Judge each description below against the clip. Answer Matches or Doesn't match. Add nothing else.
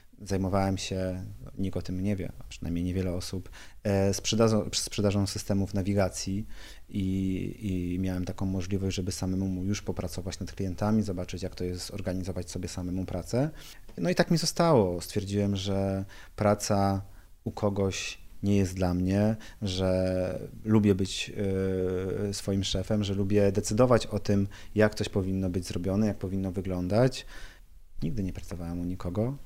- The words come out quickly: Doesn't match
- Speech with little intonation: Matches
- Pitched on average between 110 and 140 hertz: Doesn't match